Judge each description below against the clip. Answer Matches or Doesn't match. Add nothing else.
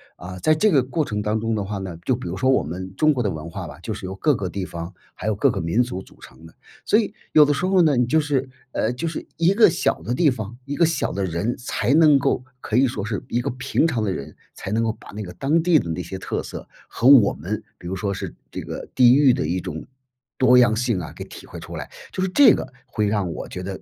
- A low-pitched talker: Matches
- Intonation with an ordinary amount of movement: Doesn't match